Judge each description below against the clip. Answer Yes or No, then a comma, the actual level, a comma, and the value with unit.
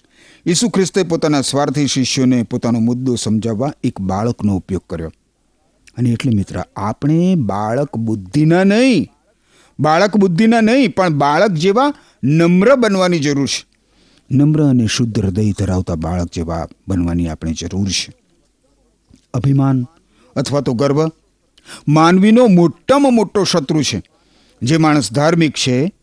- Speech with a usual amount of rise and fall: No, wide, 7.6 semitones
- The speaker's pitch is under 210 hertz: Yes, medium, 140 Hz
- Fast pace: No, average, 120 wpm